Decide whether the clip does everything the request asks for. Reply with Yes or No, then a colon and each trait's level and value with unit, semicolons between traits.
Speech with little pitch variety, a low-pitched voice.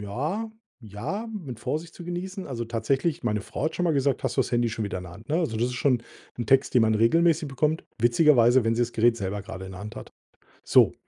No: wide, 5.8 semitones; low, 120 Hz